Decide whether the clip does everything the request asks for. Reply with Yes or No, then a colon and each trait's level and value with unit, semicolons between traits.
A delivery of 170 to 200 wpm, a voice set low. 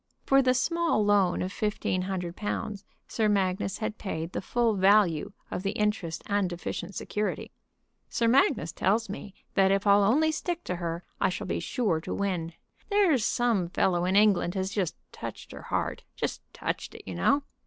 No: average, 175 wpm; high, 200 Hz